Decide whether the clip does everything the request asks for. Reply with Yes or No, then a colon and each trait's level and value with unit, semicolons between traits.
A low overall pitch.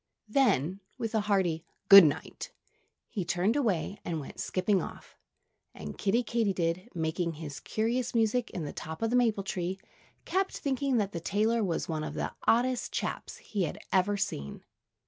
No: high, 195 Hz